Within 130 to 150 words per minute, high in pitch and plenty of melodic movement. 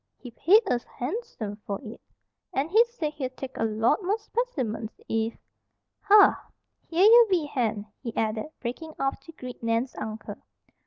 No: average, 160 wpm; very high, 260 Hz; wide, 8.2 semitones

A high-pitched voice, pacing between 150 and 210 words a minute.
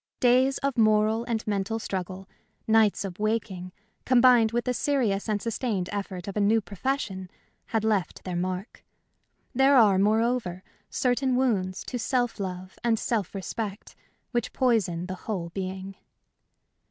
No: high, 215 Hz; average, 140 wpm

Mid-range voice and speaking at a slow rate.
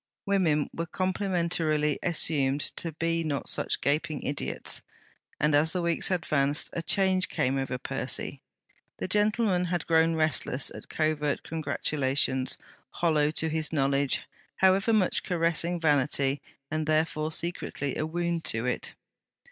Yes: medium, 160 Hz; slow, 130 wpm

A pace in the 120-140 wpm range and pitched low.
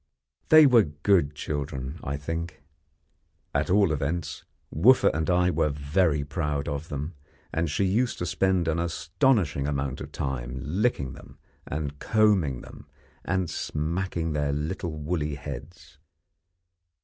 Yes: slow, 135 wpm; very low, 75 Hz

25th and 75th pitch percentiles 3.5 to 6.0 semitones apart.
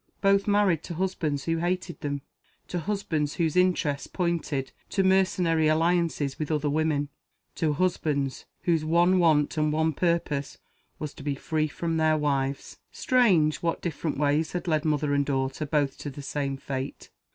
No: average, 3.1 semitones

